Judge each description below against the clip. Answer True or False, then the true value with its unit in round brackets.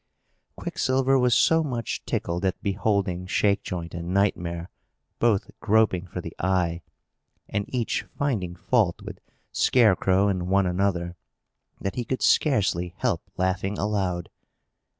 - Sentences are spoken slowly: True (125 wpm)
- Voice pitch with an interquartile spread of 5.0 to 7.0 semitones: False (3.8 semitones)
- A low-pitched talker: True (95 Hz)